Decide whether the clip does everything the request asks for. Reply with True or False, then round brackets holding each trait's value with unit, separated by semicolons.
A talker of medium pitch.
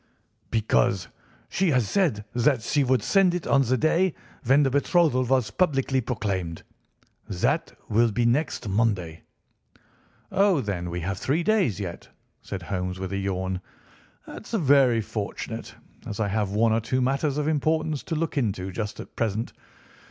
False (120 Hz)